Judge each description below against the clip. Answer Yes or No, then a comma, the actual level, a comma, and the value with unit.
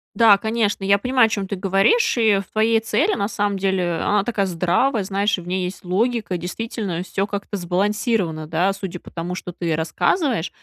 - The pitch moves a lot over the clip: No, average, 3.4 semitones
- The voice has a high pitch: Yes, high, 195 Hz